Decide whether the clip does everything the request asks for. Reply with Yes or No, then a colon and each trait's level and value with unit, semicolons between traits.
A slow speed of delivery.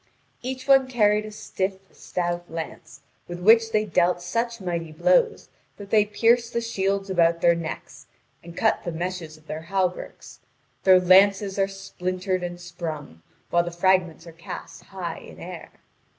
No: average, 160 wpm